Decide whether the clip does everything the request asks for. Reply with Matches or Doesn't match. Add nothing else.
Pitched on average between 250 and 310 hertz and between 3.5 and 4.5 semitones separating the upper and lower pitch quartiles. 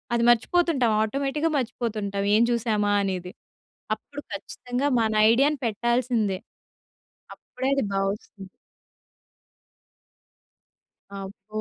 Doesn't match